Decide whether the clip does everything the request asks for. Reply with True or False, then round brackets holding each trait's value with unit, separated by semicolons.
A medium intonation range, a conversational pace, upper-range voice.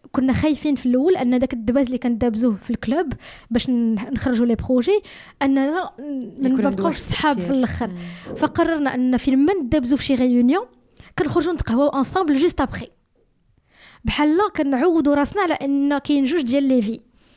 False (3.4 semitones; 155 wpm; 270 Hz)